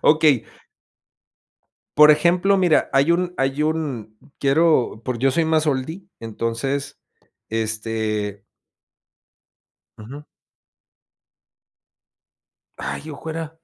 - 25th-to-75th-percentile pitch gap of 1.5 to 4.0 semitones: No, wide, 5.7 semitones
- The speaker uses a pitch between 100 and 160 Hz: Yes, medium, 140 Hz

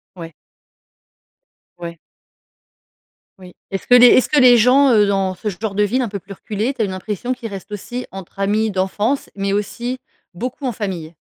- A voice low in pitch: No, high, 210 Hz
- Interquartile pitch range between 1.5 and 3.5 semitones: No, average, 4.1 semitones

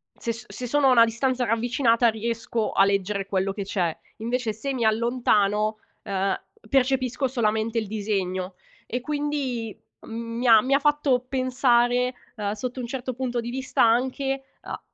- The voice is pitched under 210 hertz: No, high, 235 Hz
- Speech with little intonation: No, average, 3.0 semitones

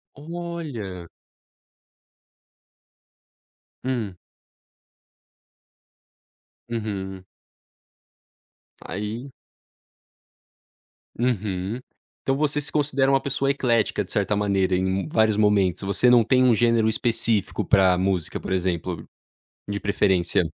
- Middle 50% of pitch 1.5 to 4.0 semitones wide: No, average, 5.1 semitones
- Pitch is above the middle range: No, low, 110 Hz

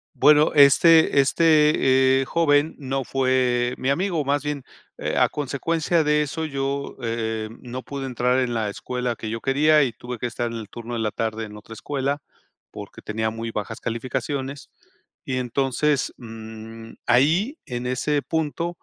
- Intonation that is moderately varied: Yes, average, 3.8 semitones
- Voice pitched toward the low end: Yes, low, 130 Hz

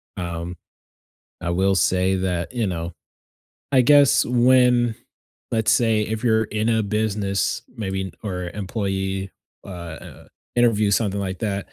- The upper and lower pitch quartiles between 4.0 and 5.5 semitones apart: No, average, 3.1 semitones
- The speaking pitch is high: No, low, 100 Hz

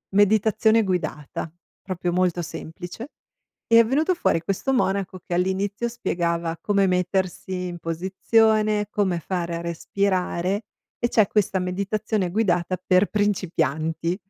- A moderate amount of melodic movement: Yes, average, 3.2 semitones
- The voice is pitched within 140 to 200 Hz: Yes, medium, 185 Hz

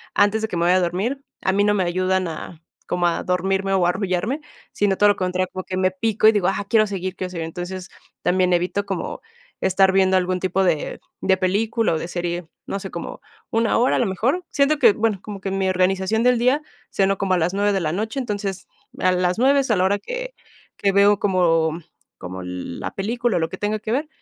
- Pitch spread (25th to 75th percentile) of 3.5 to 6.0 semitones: No, narrow, 2.5 semitones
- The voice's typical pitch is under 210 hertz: Yes, high, 190 Hz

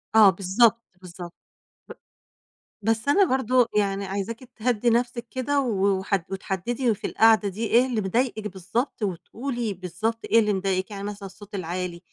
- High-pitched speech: Yes, high, 210 Hz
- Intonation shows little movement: No, average, 3.7 semitones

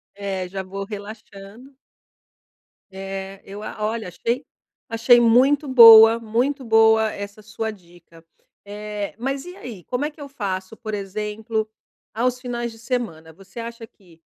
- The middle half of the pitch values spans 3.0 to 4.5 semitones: Yes, average, 3.3 semitones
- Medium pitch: No, high, 220 Hz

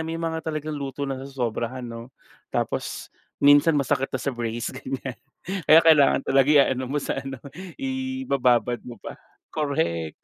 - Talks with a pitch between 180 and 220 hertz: No, low, 135 Hz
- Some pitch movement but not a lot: Yes, average, 3.9 semitones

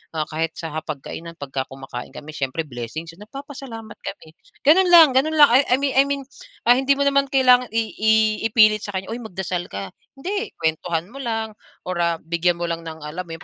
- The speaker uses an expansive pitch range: Yes, wide, 8.6 semitones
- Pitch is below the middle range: No, high, 195 Hz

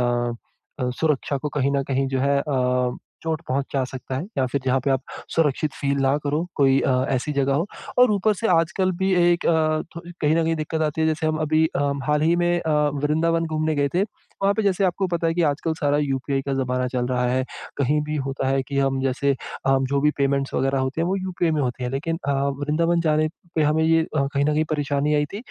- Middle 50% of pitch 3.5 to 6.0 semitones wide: No, average, 3.1 semitones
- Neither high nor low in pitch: Yes, medium, 145 Hz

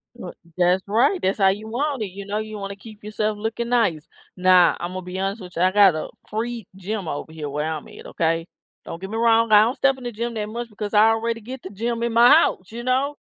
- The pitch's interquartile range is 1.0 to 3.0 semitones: No, average, 3.8 semitones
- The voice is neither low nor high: No, high, 210 Hz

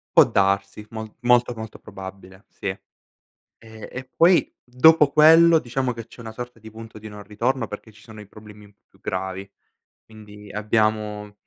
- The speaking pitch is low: Yes, low, 110 Hz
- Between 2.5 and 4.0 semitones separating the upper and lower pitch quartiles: Yes, average, 2.8 semitones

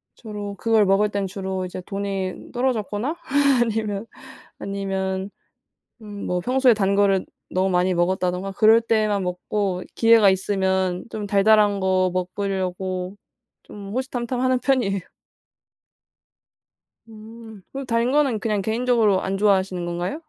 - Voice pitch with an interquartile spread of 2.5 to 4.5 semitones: Yes, average, 2.9 semitones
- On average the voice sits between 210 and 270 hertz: No, high, 200 Hz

